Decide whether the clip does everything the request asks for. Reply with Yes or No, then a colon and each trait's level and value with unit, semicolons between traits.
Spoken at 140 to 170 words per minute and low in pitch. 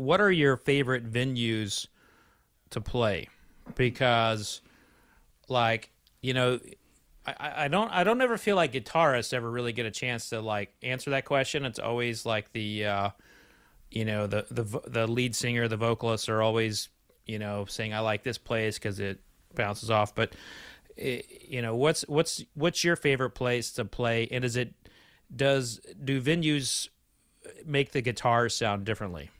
Yes: average, 160 wpm; low, 120 Hz